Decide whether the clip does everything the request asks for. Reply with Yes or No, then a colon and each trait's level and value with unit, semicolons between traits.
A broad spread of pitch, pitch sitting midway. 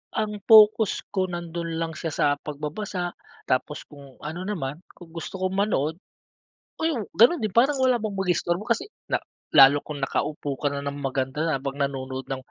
Yes: wide, 6.2 semitones; medium, 165 Hz